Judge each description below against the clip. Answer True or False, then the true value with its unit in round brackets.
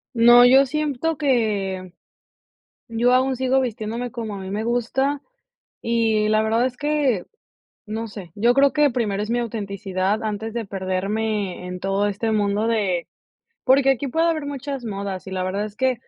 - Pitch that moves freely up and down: False (4.1 semitones)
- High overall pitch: True (225 Hz)